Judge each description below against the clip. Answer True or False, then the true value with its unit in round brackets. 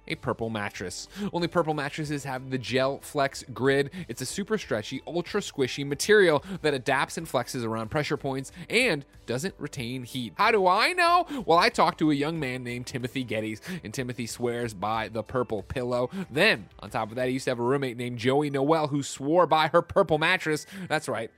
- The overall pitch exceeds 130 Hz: True (140 Hz)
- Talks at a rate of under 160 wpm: False (200 wpm)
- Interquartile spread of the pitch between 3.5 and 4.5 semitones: False (4.9 semitones)